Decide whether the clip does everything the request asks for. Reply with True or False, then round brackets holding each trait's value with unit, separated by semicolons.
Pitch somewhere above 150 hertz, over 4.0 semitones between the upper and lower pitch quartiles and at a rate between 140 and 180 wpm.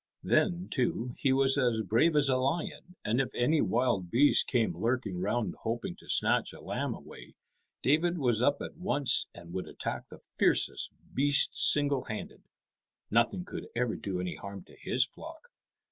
False (125 Hz; 4.5 semitones; 170 wpm)